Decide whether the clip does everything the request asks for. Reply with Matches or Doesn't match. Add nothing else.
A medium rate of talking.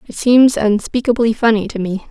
Matches